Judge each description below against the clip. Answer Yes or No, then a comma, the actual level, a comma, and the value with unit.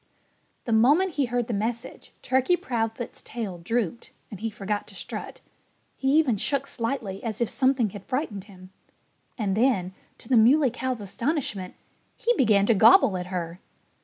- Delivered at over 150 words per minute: Yes, average, 160 wpm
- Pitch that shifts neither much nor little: Yes, average, 4.5 semitones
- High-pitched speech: Yes, high, 230 Hz